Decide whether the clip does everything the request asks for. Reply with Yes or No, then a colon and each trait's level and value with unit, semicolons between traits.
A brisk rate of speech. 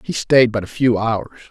Yes: fast, 240 wpm